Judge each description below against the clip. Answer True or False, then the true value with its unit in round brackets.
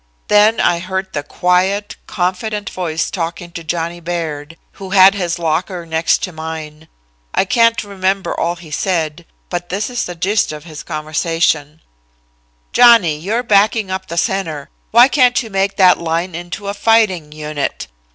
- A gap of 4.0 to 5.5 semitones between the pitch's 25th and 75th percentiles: False (3.6 semitones)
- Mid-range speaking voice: True (180 Hz)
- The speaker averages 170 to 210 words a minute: False (160 wpm)